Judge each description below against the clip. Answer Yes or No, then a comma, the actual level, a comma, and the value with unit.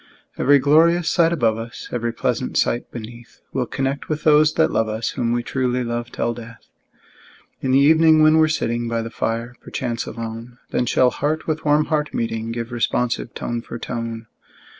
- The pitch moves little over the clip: No, average, 4.4 semitones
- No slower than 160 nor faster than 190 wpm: Yes, average, 185 wpm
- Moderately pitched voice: No, low, 120 Hz